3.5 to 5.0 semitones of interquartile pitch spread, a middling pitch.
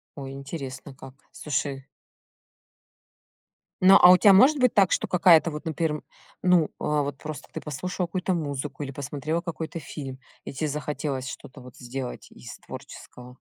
Yes: average, 4.0 semitones; medium, 150 Hz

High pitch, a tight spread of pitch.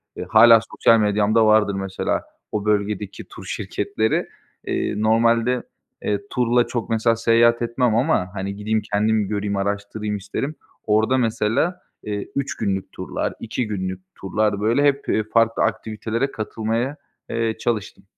No: low, 110 Hz; narrow, 2.1 semitones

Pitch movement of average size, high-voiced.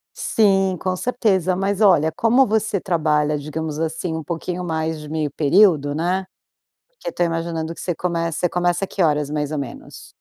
No: average, 3.4 semitones; medium, 170 Hz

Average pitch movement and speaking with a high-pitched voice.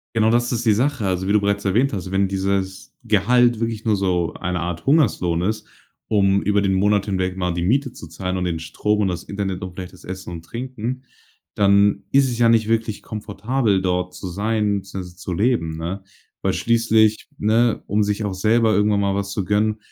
No: average, 3.0 semitones; low, 100 Hz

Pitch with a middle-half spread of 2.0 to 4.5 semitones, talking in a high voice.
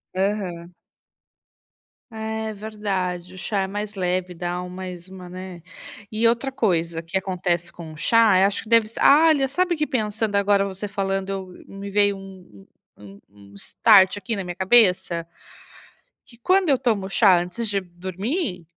Yes: average, 3.4 semitones; high, 195 Hz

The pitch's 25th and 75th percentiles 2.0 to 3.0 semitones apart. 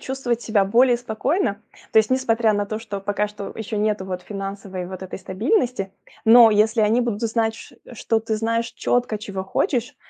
Yes: average, 2.7 semitones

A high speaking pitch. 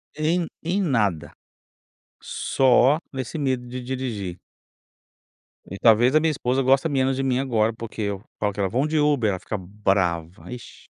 No: low, 125 Hz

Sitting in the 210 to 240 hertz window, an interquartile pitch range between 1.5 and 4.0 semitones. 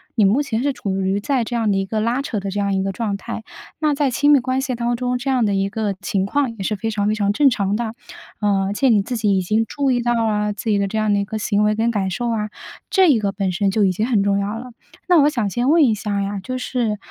Yes: high, 215 Hz; average, 3.6 semitones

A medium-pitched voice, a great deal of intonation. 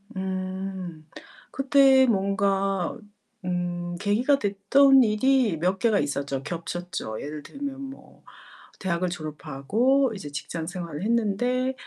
No: high, 195 Hz; wide, 6.2 semitones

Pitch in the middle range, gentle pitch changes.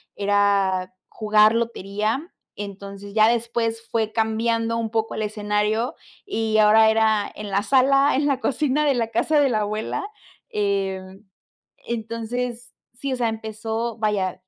No: high, 220 Hz; narrow, 2.1 semitones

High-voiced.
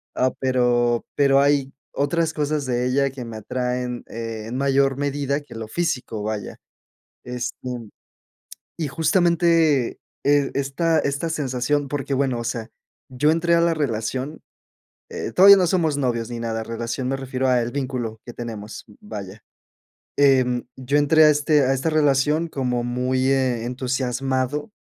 No: low, 135 Hz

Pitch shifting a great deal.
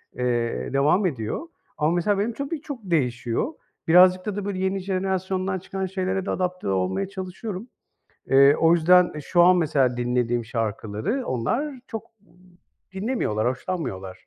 Yes: wide, 7.5 semitones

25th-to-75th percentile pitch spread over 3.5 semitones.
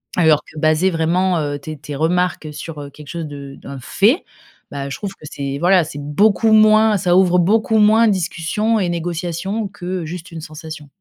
Yes: average, 4.2 semitones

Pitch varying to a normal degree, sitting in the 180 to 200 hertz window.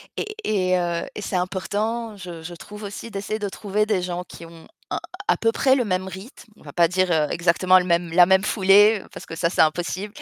Yes: average, 3.2 semitones; medium, 185 Hz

